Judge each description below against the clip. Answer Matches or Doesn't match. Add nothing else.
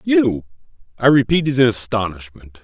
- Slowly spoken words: Matches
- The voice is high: Doesn't match